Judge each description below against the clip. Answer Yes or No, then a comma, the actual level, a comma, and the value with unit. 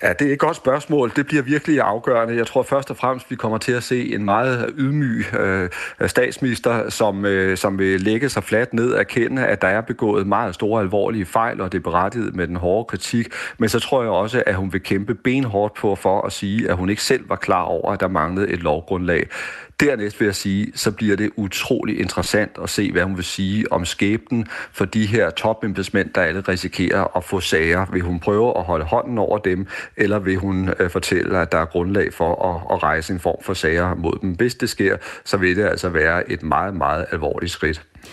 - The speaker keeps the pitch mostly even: No, average, 3.9 semitones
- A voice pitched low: Yes, low, 105 Hz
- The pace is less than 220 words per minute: No, fast, 225 wpm